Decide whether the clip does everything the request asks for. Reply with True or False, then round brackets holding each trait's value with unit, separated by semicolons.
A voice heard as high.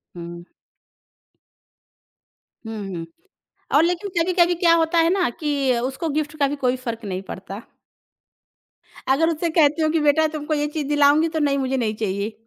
True (290 Hz)